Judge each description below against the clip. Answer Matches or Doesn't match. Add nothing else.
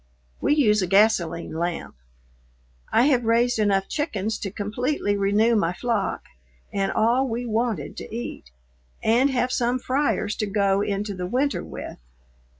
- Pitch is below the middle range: Doesn't match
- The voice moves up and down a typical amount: Matches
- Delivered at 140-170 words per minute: Matches